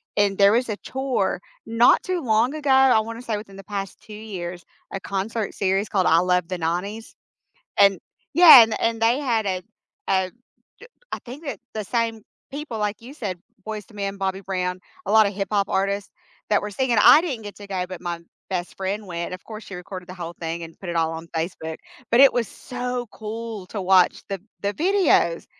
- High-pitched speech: Yes, high, 205 Hz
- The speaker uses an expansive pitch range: No, average, 3.7 semitones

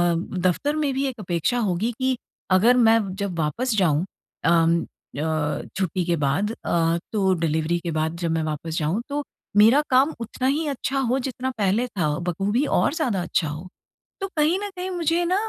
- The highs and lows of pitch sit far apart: Yes, wide, 7.8 semitones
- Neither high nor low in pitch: No, high, 200 Hz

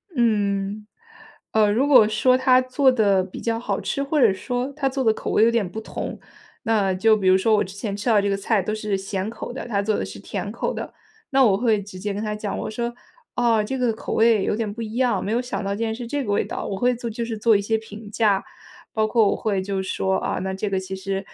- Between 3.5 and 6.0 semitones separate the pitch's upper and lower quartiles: No, average, 2.9 semitones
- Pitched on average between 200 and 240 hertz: Yes, high, 215 Hz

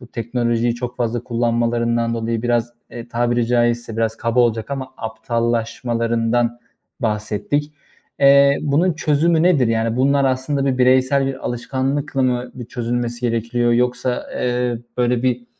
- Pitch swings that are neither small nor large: No, narrow, 1.9 semitones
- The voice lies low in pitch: Yes, low, 120 Hz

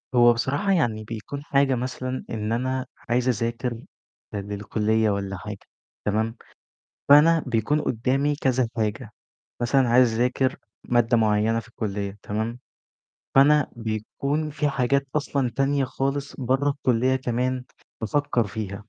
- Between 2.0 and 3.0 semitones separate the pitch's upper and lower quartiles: No, average, 3.7 semitones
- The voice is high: No, low, 125 Hz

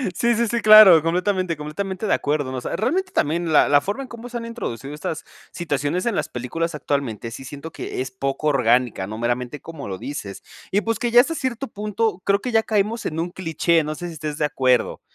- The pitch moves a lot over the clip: Yes, wide, 7.4 semitones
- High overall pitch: No, medium, 165 Hz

